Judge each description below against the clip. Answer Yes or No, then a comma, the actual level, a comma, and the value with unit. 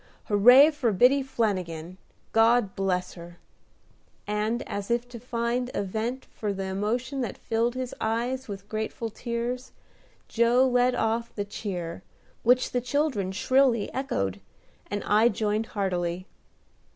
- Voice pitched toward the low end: No, high, 225 Hz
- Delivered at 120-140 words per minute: Yes, slow, 135 wpm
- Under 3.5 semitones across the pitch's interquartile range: No, average, 3.8 semitones